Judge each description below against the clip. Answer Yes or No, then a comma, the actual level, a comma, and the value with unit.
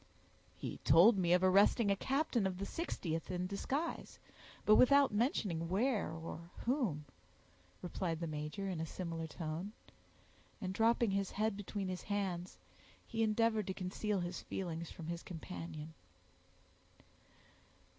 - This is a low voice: No, high, 190 Hz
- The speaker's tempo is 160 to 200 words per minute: No, slow, 135 wpm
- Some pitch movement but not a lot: Yes, average, 4.1 semitones